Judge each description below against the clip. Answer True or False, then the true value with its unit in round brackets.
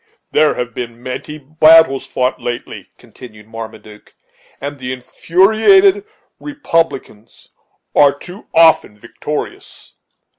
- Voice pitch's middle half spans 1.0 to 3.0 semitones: False (5.5 semitones)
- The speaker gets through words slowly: True (100 wpm)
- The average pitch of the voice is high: False (140 Hz)